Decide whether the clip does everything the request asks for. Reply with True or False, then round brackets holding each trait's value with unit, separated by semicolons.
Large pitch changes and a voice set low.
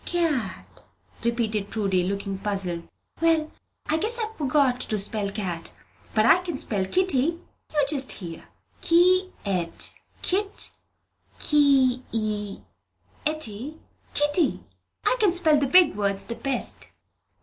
False (8.2 semitones; 260 Hz)